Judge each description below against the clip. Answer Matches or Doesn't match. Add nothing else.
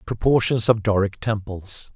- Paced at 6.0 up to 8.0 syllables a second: Doesn't match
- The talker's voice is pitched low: Matches